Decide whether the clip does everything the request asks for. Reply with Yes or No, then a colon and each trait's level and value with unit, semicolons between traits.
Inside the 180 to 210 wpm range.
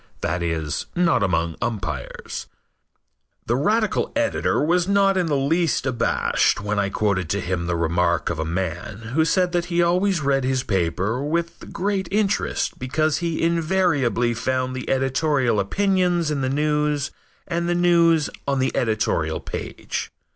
No: average, 155 wpm